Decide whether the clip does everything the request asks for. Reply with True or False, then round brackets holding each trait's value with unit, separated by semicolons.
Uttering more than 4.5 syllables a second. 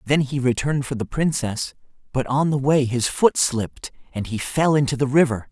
True (5.2 syllables/s)